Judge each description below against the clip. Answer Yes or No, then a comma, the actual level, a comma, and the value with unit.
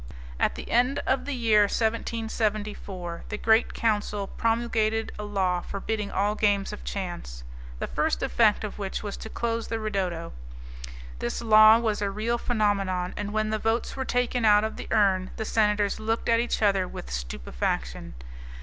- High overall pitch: Yes, high, 210 Hz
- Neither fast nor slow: Yes, average, 170 wpm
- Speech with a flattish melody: Yes, narrow, 2.3 semitones